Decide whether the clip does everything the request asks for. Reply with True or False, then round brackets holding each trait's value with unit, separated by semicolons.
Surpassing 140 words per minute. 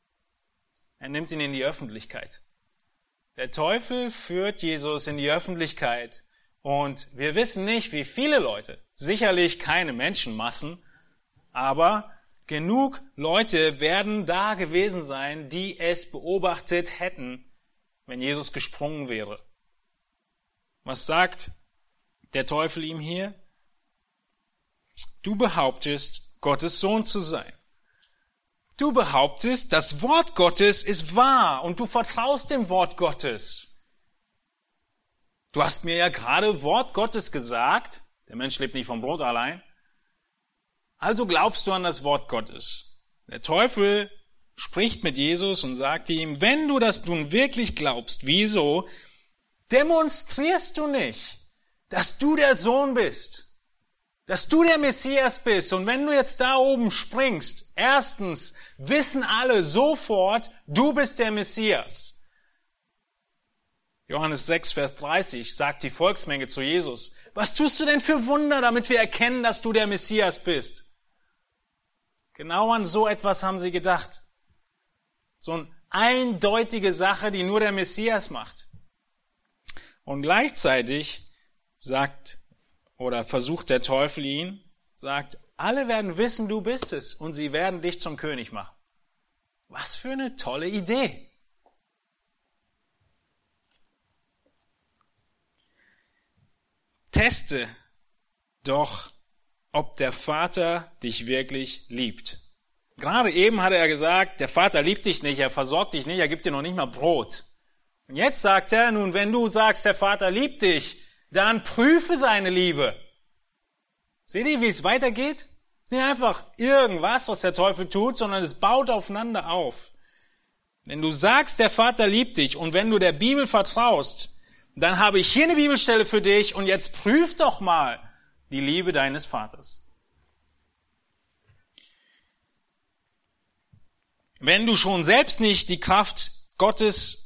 False (130 wpm)